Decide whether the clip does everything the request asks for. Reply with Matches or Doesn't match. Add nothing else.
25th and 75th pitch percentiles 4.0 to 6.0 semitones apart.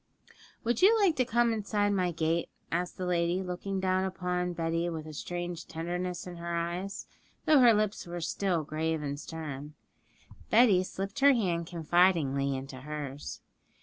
Doesn't match